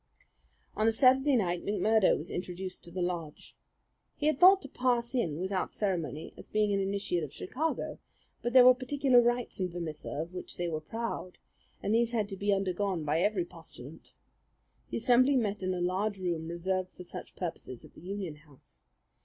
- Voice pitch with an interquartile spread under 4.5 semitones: No, average, 5.2 semitones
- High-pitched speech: Yes, high, 195 Hz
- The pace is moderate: Yes, average, 185 wpm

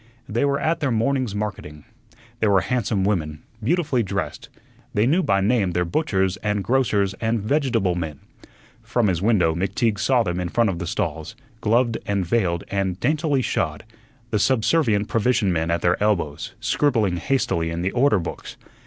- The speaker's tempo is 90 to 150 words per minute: No, average, 170 wpm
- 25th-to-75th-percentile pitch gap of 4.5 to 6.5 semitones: Yes, wide, 5.4 semitones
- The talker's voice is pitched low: Yes, low, 105 Hz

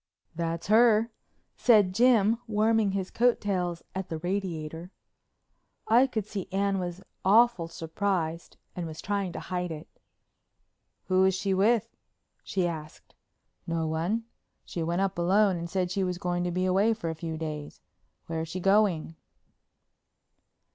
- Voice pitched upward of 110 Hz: Yes, medium, 185 Hz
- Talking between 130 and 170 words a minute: Yes, average, 150 wpm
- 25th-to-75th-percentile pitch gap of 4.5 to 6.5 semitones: No, average, 3.6 semitones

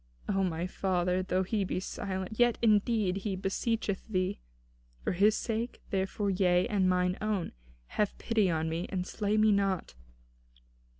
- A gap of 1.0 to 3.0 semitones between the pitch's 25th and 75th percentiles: Yes, narrow, 2.5 semitones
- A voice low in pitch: No, high, 195 Hz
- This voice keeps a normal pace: Yes, average, 160 wpm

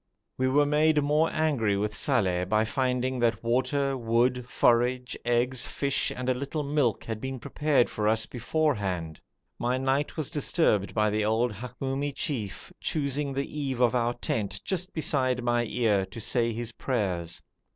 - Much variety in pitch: No, average, 3.8 semitones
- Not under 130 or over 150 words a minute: No, average, 160 wpm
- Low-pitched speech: Yes, low, 125 Hz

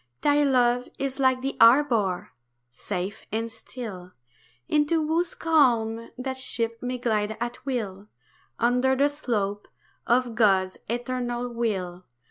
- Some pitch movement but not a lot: Yes, average, 3.2 semitones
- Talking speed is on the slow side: Yes, slow, 120 wpm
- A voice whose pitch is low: No, high, 240 Hz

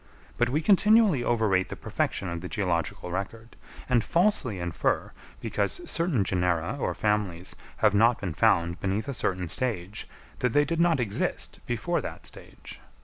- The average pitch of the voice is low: Yes, low, 105 Hz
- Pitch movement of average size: No, wide, 5.9 semitones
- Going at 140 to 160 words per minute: Yes, average, 155 wpm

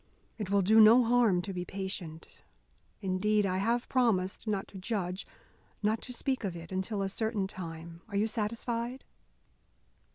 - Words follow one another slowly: No, average, 160 wpm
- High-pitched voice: Yes, high, 200 Hz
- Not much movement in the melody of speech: No, average, 3.3 semitones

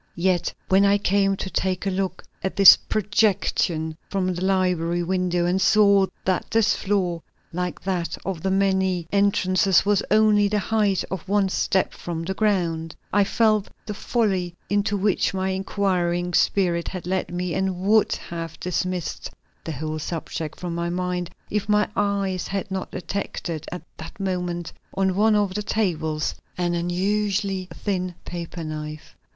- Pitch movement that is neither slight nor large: No, narrow, 2.3 semitones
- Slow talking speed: No, average, 155 wpm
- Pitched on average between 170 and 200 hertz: Yes, medium, 185 Hz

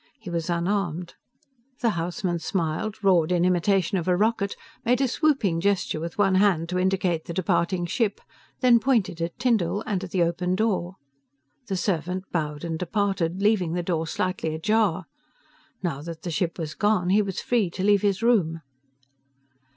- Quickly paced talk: No, average, 170 wpm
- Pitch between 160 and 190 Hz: Yes, medium, 185 Hz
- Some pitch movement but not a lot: Yes, average, 3.2 semitones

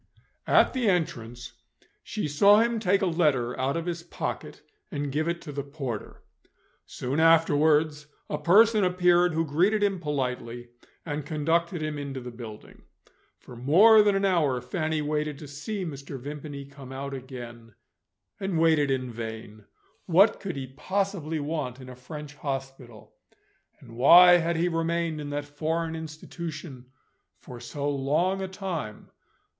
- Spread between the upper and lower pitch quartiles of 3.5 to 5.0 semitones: Yes, average, 4.2 semitones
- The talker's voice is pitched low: No, medium, 150 Hz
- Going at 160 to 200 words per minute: No, average, 150 wpm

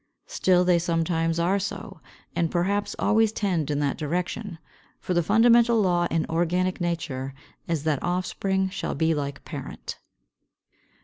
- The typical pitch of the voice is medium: Yes, medium, 175 Hz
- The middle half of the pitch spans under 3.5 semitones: Yes, average, 3.1 semitones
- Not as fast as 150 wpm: Yes, average, 140 wpm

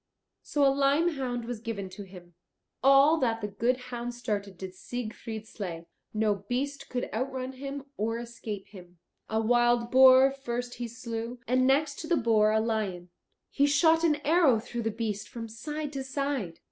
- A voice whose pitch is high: Yes, high, 240 Hz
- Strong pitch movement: No, average, 3.9 semitones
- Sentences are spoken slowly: No, average, 175 wpm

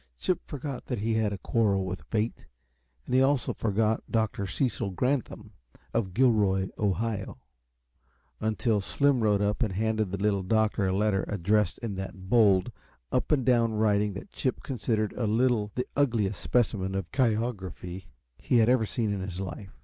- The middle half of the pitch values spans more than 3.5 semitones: No, average, 3.2 semitones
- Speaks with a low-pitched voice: Yes, low, 105 Hz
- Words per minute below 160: No, average, 165 wpm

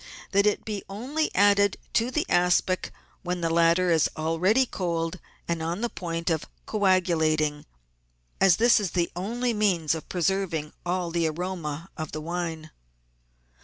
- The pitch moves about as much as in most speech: Yes, average, 3.5 semitones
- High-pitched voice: No, medium, 175 Hz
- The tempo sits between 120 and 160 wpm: Yes, average, 150 wpm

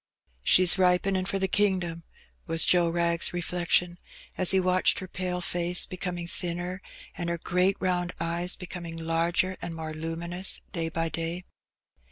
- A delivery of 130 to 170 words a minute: Yes, average, 155 wpm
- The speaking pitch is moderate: Yes, medium, 175 Hz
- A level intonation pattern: Yes, narrow, 1.5 semitones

